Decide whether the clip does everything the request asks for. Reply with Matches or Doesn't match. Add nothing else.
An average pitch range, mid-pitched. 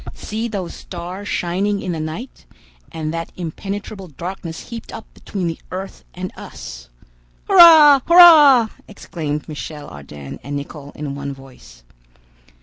Doesn't match